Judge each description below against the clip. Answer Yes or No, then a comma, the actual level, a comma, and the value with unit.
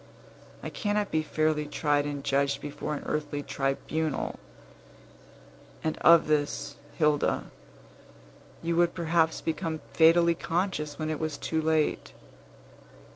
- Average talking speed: No, slow, 120 wpm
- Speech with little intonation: Yes, narrow, 2.0 semitones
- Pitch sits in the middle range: Yes, medium, 155 Hz